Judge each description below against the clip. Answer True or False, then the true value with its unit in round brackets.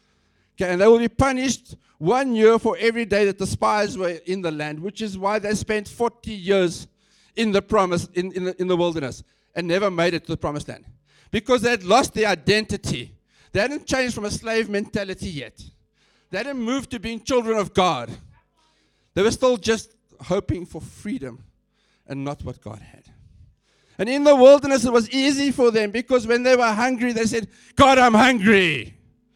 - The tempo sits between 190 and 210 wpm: True (195 wpm)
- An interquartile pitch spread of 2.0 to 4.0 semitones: False (4.9 semitones)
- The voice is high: True (210 Hz)